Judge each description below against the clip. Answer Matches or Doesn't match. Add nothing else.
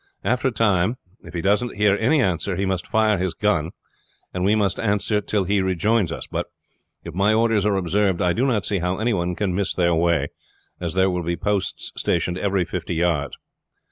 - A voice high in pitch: Doesn't match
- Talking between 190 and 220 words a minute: Matches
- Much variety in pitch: Doesn't match